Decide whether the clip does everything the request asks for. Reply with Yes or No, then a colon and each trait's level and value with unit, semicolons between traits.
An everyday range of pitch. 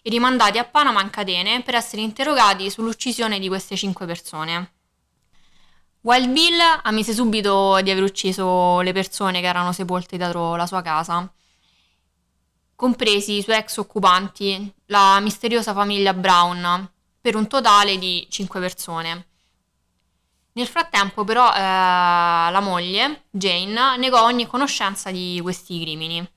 Yes: average, 3.8 semitones